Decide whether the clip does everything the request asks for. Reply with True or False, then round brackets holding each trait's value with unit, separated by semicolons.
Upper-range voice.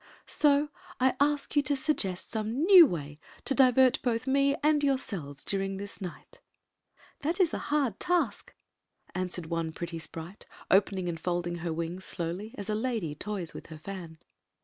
True (200 Hz)